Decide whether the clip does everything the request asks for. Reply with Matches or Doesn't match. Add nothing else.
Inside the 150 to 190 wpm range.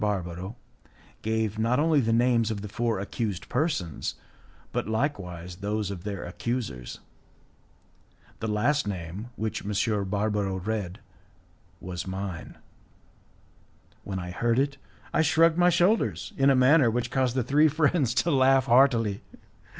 Doesn't match